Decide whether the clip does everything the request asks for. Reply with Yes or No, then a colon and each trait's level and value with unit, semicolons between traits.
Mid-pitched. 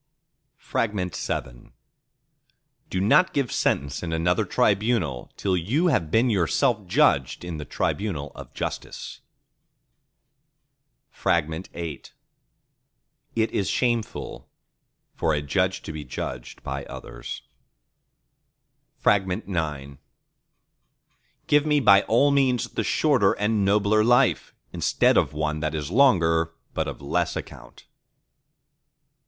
No: very low, 95 Hz